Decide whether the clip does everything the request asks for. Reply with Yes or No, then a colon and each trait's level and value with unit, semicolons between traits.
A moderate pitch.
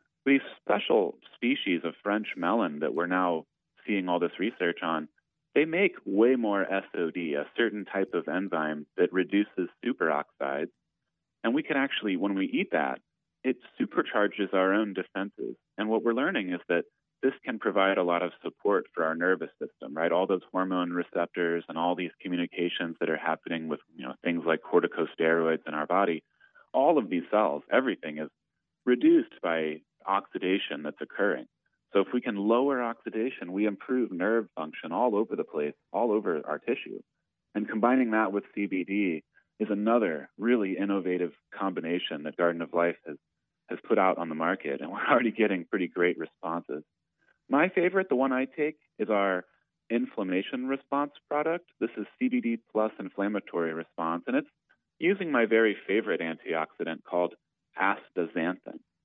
No: very low, 95 Hz